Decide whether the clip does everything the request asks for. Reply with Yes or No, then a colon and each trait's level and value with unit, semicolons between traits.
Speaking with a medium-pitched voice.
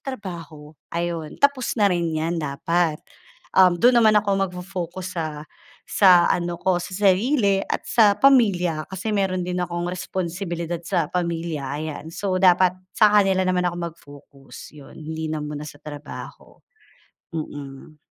Yes: medium, 175 Hz